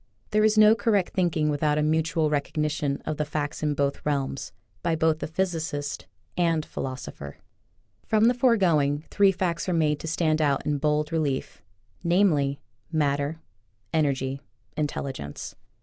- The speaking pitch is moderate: Yes, medium, 155 Hz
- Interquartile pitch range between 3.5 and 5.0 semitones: No, average, 2.9 semitones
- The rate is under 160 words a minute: Yes, average, 150 wpm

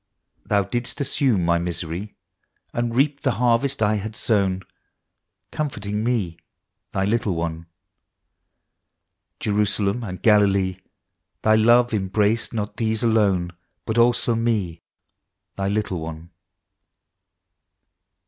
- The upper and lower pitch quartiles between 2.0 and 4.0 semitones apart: Yes, average, 3.7 semitones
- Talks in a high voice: No, low, 105 Hz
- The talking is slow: Yes, slow, 110 wpm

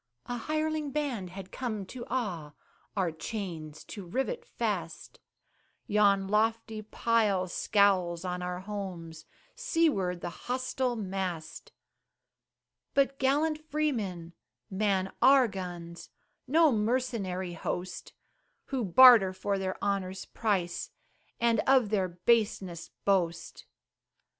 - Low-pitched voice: No, high, 200 Hz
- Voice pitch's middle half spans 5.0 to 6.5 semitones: Yes, wide, 5.5 semitones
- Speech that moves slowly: Yes, slow, 105 wpm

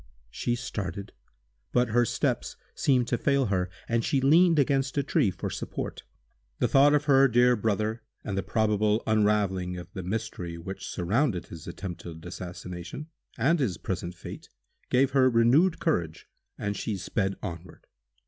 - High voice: No, low, 110 Hz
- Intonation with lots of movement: Yes, wide, 6.3 semitones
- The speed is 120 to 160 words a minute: Yes, average, 155 wpm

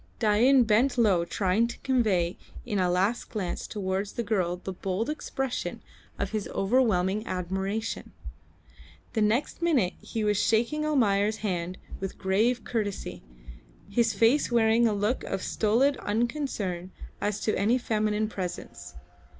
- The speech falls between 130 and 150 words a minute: Yes, slow, 135 wpm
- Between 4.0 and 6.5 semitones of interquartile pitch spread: No, average, 3.6 semitones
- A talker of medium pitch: No, high, 215 Hz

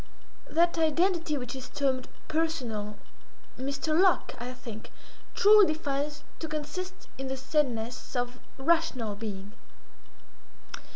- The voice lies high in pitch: Yes, very high, 280 Hz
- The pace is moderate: No, slow, 110 wpm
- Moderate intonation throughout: Yes, average, 4.8 semitones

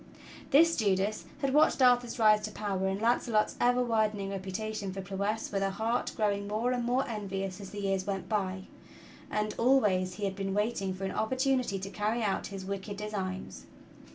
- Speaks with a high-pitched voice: Yes, high, 210 Hz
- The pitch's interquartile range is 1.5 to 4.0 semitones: Yes, average, 3.0 semitones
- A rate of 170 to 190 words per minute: Yes, average, 180 wpm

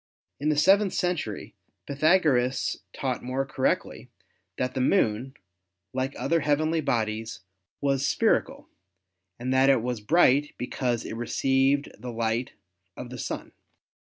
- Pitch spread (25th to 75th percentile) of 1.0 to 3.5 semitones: Yes, average, 3.1 semitones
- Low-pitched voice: Yes, low, 130 Hz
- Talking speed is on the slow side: Yes, slow, 130 wpm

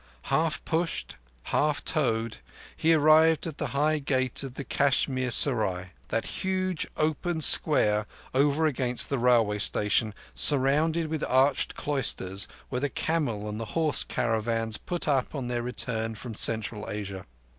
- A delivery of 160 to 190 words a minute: No, average, 140 wpm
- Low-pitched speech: Yes, low, 130 Hz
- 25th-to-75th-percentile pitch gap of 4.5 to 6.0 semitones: Yes, wide, 5.4 semitones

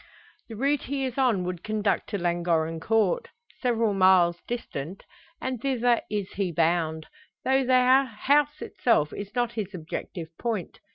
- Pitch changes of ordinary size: No, wide, 6.2 semitones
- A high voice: Yes, high, 210 Hz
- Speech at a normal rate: Yes, average, 150 wpm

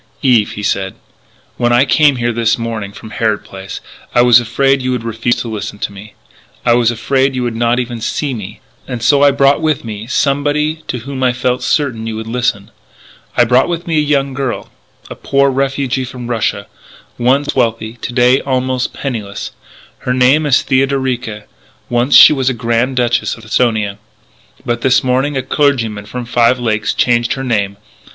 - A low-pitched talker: Yes, low, 125 Hz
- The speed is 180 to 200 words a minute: Yes, average, 185 wpm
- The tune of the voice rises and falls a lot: No, average, 2.9 semitones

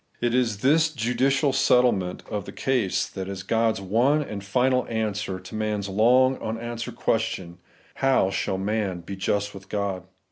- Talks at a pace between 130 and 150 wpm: No, average, 170 wpm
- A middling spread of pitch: Yes, average, 4.2 semitones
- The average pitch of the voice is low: Yes, low, 110 Hz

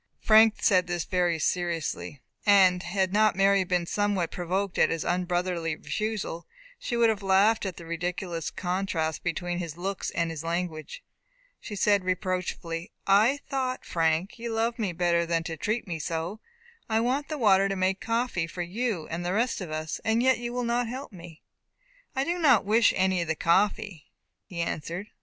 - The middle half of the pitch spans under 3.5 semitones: No, average, 4.2 semitones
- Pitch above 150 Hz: Yes, medium, 185 Hz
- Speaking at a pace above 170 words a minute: Yes, average, 180 wpm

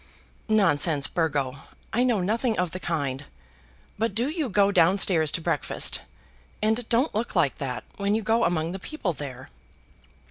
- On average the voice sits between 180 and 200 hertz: Yes, high, 190 Hz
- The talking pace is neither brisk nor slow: Yes, average, 165 wpm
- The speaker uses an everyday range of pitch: No, wide, 6.1 semitones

